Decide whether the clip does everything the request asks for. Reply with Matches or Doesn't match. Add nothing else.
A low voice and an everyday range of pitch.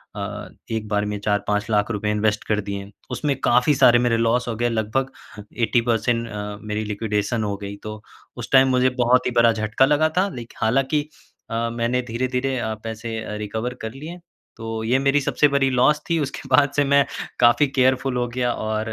Matches